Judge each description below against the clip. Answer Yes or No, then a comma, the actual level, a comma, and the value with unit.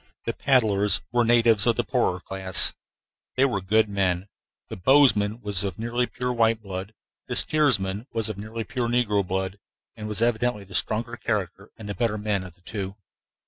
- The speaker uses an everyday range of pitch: Yes, average, 3.3 semitones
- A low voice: Yes, low, 105 Hz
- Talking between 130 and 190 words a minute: Yes, average, 180 wpm